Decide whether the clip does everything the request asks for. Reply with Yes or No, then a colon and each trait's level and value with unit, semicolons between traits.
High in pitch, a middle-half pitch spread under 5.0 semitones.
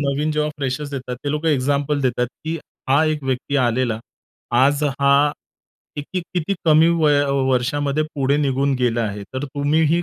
No: medium, 145 Hz; narrow, 2.5 semitones